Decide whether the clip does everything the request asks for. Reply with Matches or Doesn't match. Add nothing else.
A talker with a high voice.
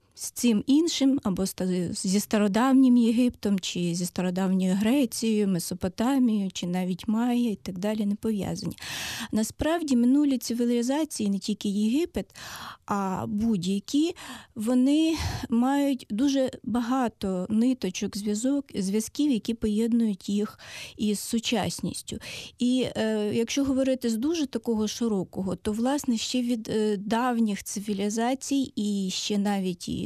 Matches